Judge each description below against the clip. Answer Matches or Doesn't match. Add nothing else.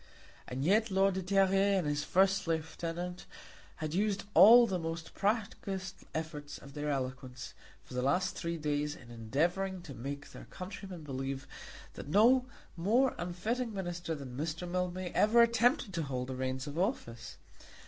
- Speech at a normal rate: Matches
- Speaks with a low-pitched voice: Doesn't match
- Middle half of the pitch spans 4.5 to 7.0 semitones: Matches